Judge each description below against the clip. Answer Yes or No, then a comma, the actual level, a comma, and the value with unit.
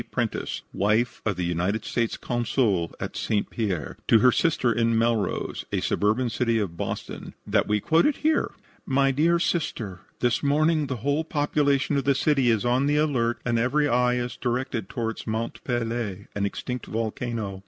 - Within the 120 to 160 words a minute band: No, average, 175 wpm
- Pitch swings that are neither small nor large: Yes, average, 4.1 semitones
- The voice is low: Yes, low, 120 Hz